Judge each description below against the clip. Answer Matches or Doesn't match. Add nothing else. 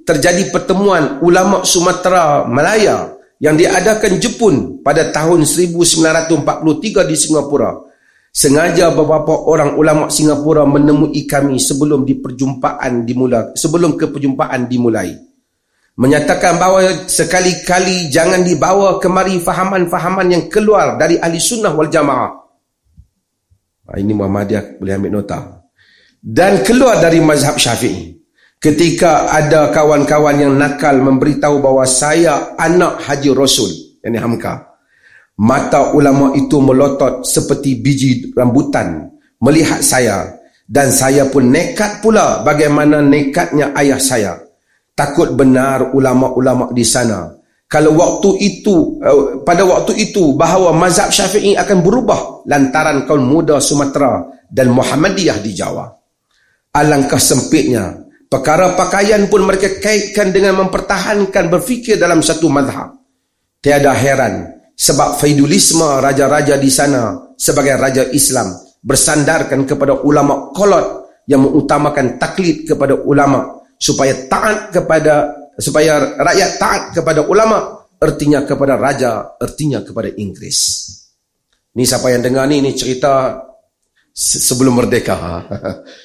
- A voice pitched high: Doesn't match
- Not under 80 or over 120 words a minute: Matches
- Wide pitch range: Doesn't match